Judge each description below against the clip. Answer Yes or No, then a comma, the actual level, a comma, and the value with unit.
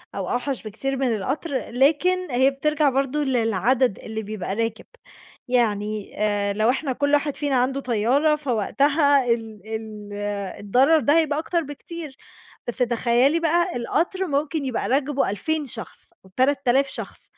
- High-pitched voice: Yes, very high, 265 Hz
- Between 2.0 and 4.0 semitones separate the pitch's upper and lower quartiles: No, average, 4.5 semitones